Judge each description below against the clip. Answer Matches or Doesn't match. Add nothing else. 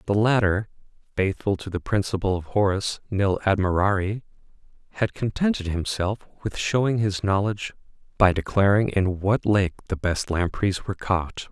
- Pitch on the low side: Matches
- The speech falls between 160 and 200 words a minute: Doesn't match